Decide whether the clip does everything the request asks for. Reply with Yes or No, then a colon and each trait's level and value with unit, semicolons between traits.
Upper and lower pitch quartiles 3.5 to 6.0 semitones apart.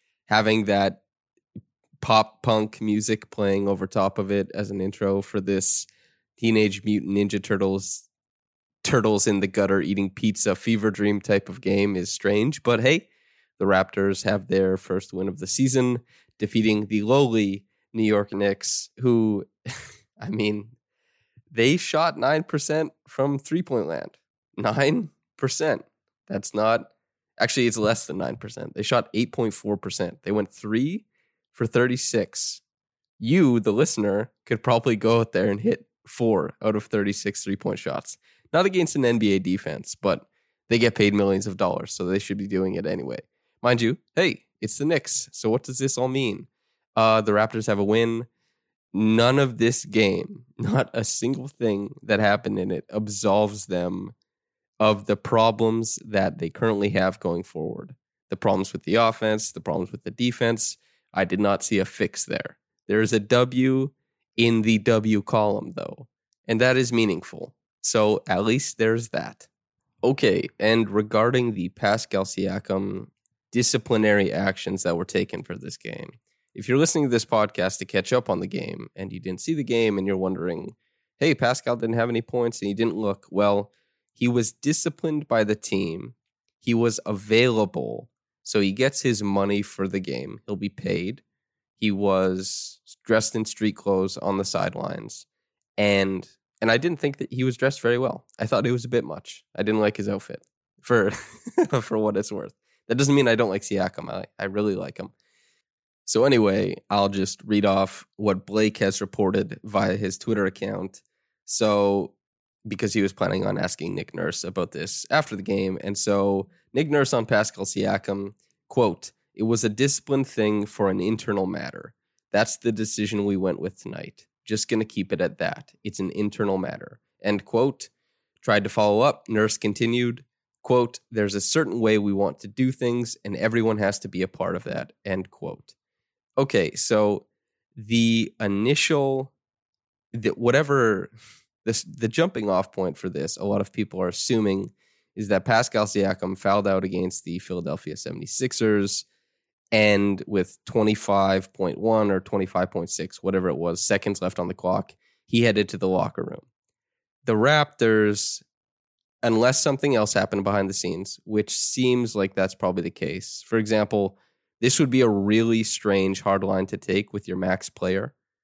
No: average, 2.9 semitones